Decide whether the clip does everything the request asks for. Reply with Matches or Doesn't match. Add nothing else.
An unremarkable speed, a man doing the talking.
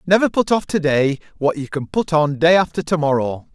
Doesn't match